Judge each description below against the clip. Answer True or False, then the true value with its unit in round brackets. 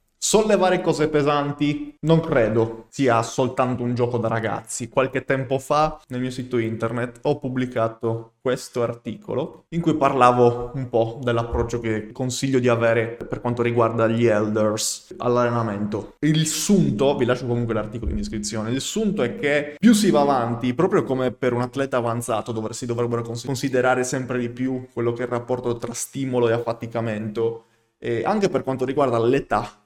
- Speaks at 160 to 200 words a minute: True (165 wpm)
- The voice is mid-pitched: False (120 Hz)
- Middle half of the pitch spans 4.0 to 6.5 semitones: False (2.9 semitones)